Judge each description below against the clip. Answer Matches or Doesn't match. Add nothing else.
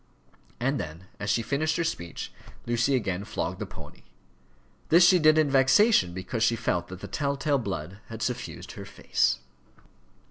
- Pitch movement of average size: Doesn't match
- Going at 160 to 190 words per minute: Matches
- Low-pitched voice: Matches